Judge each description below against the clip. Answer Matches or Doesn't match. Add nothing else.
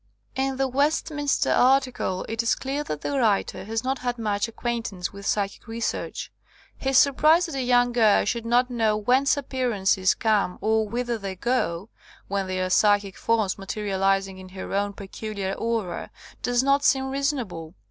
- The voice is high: Matches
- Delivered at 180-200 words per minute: Doesn't match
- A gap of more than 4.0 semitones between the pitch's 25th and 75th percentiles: Matches